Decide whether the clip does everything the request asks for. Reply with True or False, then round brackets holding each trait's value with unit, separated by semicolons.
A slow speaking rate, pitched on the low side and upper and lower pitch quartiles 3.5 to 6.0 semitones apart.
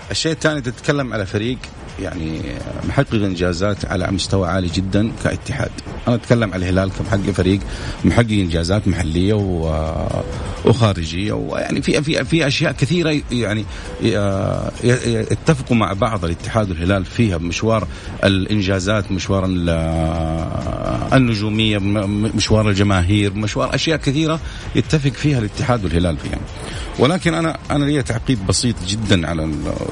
True (115 wpm; 105 Hz; 4.5 semitones)